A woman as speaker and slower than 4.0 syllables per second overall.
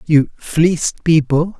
No: male; 3.7 syllables/s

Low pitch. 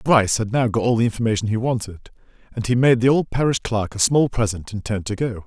Yes: low, 115 Hz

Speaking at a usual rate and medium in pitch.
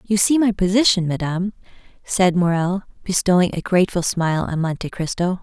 Yes: average, 155 wpm; medium, 180 Hz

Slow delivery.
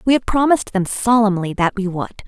No: fast, 210 wpm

